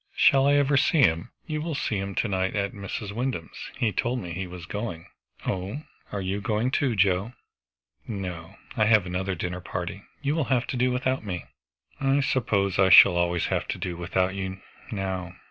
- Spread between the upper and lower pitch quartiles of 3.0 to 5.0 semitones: No, wide, 5.4 semitones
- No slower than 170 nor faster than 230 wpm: Yes, average, 195 wpm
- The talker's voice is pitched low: Yes, low, 100 Hz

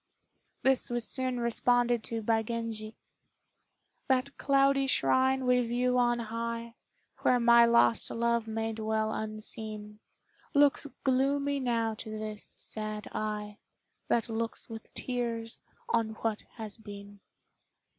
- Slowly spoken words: Yes, slow, 120 wpm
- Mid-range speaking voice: No, high, 230 Hz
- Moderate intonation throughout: No, narrow, 2.3 semitones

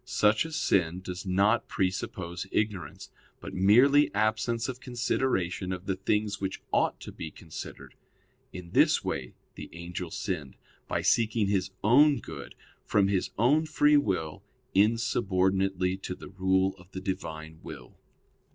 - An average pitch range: Yes, average, 3.8 semitones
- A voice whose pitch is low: Yes, very low, 95 Hz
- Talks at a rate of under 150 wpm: Yes, average, 140 wpm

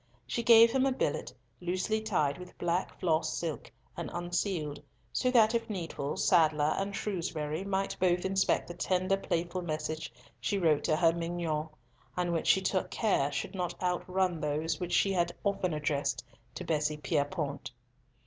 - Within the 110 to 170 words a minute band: Yes, average, 160 wpm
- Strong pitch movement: No, average, 3.7 semitones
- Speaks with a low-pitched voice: No, medium, 175 Hz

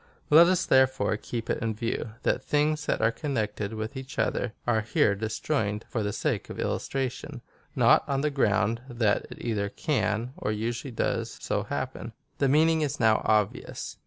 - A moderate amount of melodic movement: Yes, average, 4.1 semitones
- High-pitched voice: No, low, 120 Hz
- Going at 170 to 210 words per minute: Yes, average, 180 wpm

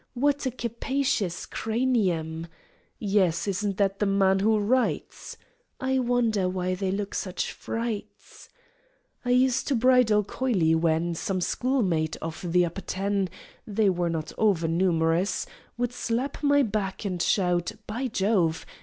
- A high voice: Yes, high, 200 Hz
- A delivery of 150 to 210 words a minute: No, slow, 135 wpm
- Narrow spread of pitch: No, average, 5.1 semitones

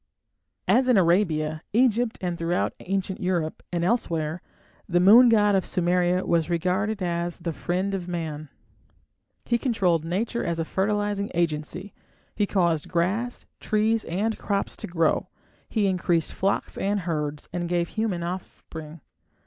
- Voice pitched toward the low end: No, medium, 180 Hz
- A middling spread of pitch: Yes, average, 3.4 semitones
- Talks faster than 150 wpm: No, average, 140 wpm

